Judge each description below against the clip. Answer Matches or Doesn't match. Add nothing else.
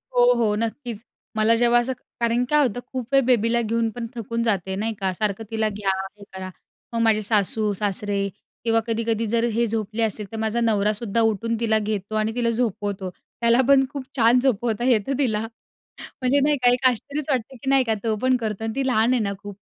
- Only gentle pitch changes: Matches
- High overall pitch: Matches